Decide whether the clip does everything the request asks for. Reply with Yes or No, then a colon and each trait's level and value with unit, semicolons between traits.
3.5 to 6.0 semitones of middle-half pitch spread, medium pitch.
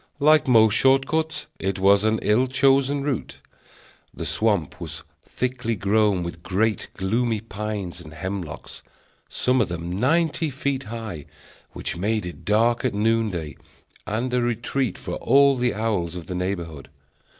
No: average, 5.2 semitones; low, 110 Hz